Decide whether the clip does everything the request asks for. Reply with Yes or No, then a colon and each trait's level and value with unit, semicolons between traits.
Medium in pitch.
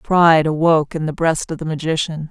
Yes: medium, 160 Hz